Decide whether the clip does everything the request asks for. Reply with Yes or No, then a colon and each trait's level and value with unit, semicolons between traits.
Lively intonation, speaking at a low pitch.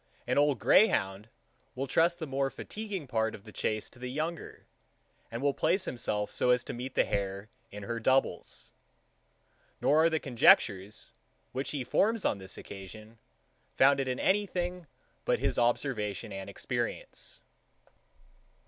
Yes: wide, 6.5 semitones; low, 125 Hz